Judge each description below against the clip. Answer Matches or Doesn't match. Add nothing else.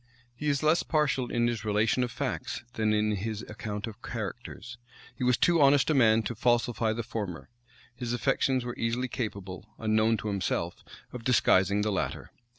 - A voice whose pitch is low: Matches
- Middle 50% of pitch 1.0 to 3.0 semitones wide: Matches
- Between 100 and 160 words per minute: Doesn't match